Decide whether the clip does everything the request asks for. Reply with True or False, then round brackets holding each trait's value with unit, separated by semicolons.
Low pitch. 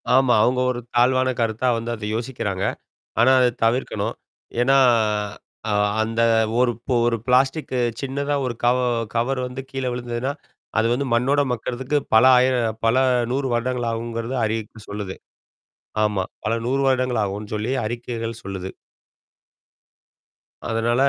True (120 Hz)